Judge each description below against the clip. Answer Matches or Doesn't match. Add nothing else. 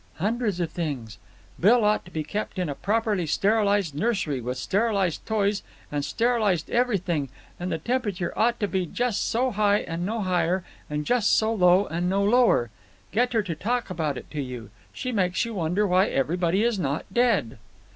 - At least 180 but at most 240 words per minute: Matches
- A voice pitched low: Doesn't match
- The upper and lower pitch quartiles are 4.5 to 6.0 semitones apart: Matches